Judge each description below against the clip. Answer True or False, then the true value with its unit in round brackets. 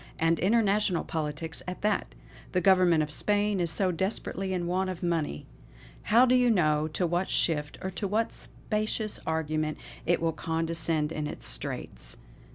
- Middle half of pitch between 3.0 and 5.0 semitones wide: True (3.9 semitones)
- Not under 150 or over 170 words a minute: True (160 wpm)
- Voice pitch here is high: False (175 Hz)